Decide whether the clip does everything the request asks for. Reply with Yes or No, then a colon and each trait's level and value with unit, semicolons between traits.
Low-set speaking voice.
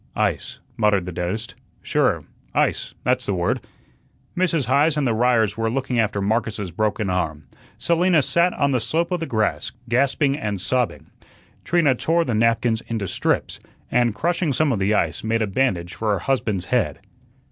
Yes: low, 115 Hz